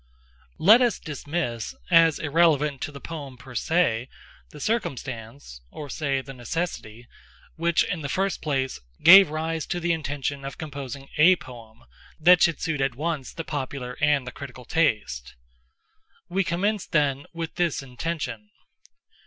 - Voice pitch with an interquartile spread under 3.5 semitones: No, average, 4.6 semitones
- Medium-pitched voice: Yes, medium, 145 Hz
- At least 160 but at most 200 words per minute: No, slow, 135 wpm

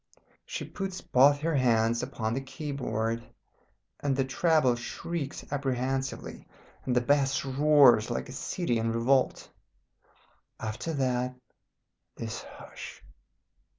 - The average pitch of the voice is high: No, low, 130 Hz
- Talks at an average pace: No, slow, 120 wpm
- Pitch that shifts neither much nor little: Yes, average, 3.2 semitones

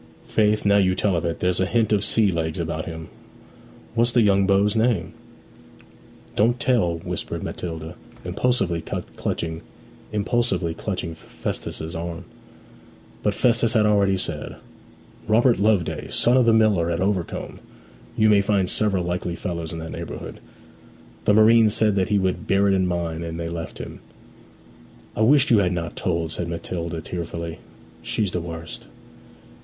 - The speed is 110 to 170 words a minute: Yes, average, 150 wpm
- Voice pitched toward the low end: Yes, very low, 95 Hz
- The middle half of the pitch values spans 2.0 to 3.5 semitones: No, average, 4.2 semitones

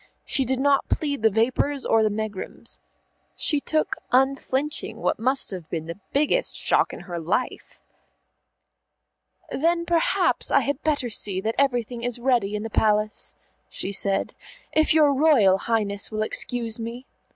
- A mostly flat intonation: No, average, 4.9 semitones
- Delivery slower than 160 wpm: Yes, average, 150 wpm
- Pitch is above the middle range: Yes, high, 240 Hz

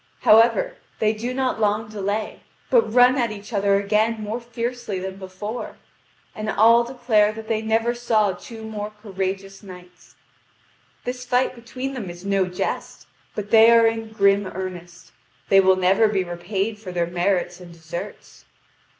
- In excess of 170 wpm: No, average, 160 wpm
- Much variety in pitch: No, average, 3.2 semitones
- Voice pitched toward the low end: No, high, 210 Hz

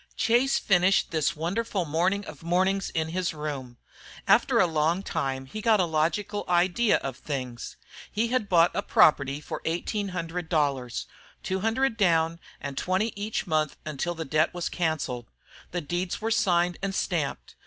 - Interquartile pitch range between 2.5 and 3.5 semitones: No, average, 4.3 semitones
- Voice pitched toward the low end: No, medium, 175 Hz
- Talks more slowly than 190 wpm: Yes, average, 165 wpm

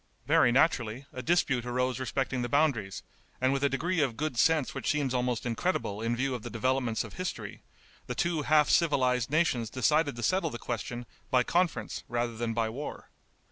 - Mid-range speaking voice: No, low, 130 Hz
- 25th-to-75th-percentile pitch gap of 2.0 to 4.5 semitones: Yes, average, 4.1 semitones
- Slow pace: No, average, 185 wpm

